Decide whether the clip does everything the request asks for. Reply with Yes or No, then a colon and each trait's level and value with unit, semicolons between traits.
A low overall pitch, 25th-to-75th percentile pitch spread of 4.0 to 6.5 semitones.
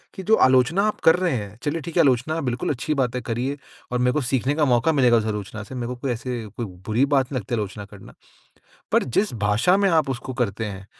Yes: low, 125 Hz; average, 4.4 semitones